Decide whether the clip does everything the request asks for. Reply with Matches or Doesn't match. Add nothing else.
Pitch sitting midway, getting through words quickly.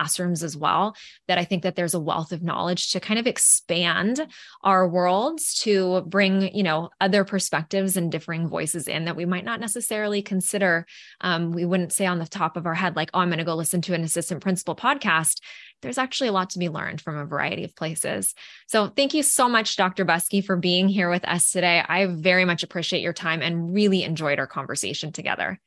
Matches